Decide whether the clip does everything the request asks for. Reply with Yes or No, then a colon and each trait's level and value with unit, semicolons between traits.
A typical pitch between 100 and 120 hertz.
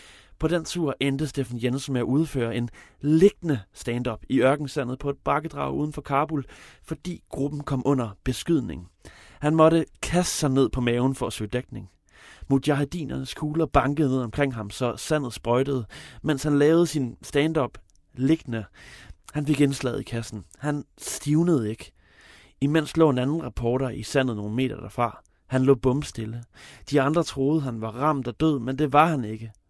No: low, 135 Hz